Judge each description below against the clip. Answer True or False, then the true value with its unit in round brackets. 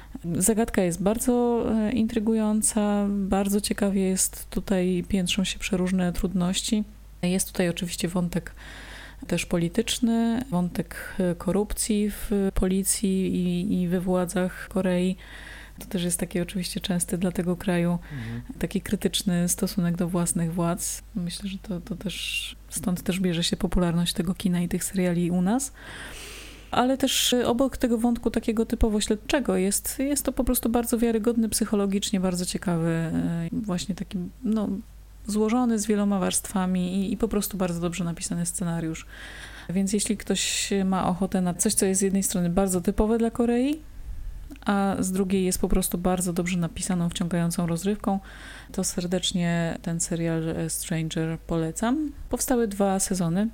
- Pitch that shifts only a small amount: False (3.1 semitones)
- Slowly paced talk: False (145 wpm)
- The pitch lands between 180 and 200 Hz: True (190 Hz)